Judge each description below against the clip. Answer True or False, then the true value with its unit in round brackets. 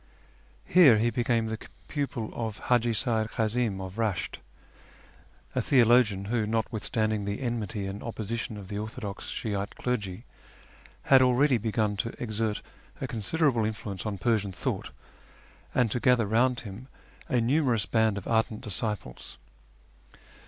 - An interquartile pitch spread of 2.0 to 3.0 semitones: True (2.7 semitones)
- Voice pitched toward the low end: True (110 Hz)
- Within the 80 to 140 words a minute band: True (135 wpm)